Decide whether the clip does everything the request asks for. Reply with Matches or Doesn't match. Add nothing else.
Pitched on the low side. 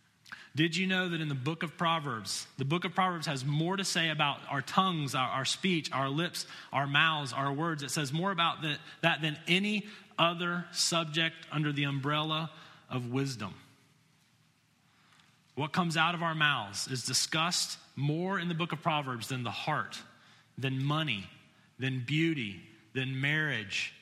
Doesn't match